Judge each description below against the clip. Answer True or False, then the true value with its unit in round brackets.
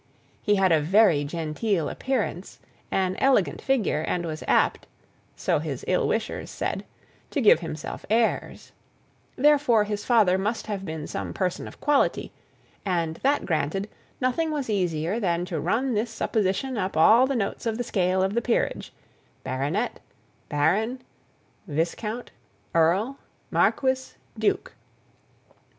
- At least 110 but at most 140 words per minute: True (135 wpm)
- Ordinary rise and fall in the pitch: False (5.9 semitones)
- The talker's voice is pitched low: False (200 Hz)